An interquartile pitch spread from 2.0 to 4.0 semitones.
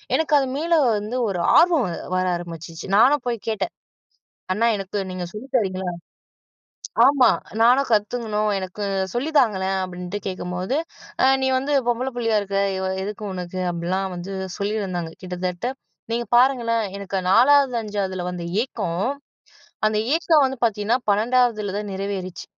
No: average, 4.7 semitones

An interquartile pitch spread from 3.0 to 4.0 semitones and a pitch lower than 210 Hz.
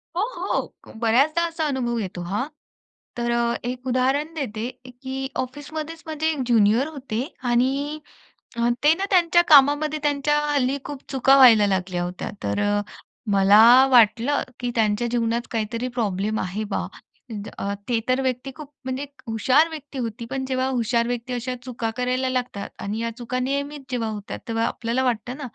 No: average, 3.6 semitones; very high, 250 Hz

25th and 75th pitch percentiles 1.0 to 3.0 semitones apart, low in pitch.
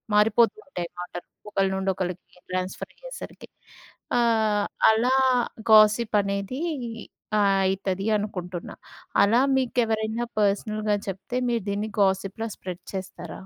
No: average, 2.7 semitones; high, 205 Hz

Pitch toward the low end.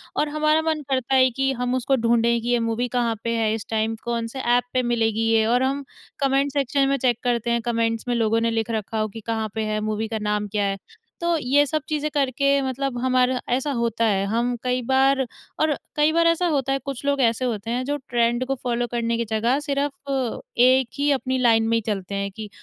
No: high, 245 Hz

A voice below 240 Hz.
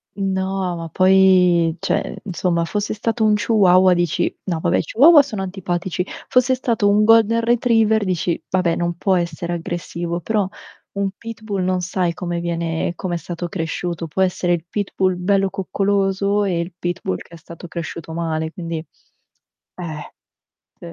Yes: medium, 185 Hz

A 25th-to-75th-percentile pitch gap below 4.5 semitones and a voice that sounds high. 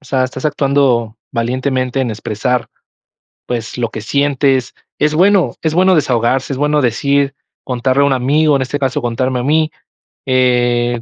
No: average, 2.8 semitones; low, 130 Hz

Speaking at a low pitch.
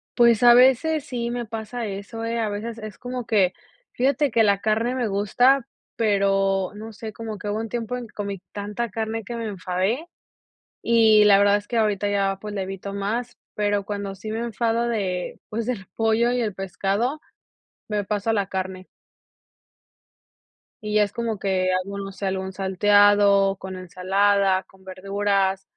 No: high, 205 Hz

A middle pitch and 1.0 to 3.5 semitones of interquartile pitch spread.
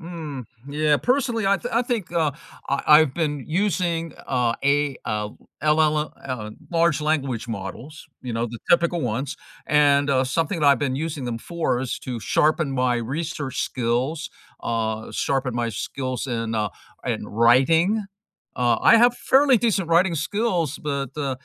No: medium, 145 Hz; average, 4.9 semitones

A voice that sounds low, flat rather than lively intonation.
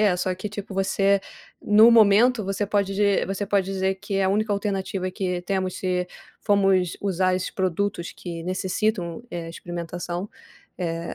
No: high, 190 Hz; narrow, 1.9 semitones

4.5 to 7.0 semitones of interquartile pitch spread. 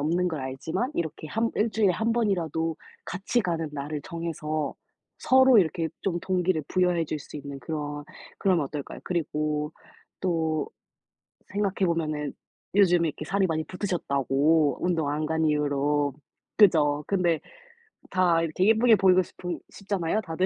No: average, 3.6 semitones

